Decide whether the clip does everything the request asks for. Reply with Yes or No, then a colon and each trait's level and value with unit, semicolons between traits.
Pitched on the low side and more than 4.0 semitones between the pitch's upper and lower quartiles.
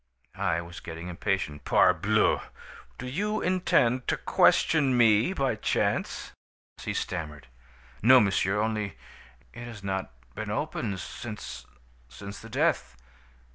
Yes: low, 105 Hz; average, 5.2 semitones